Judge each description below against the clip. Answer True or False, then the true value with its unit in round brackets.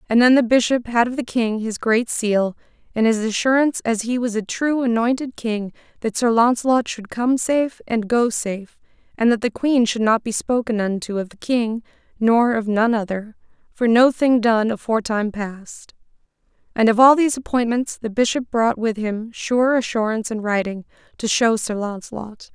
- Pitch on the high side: True (230 Hz)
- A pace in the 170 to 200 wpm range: True (190 wpm)